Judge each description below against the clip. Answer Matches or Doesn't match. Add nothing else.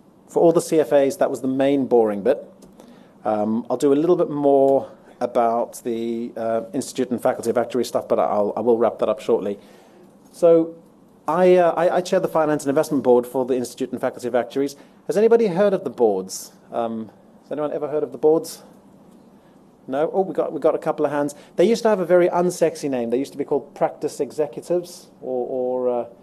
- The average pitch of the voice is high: Doesn't match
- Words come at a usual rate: Doesn't match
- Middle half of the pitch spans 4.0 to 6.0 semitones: Matches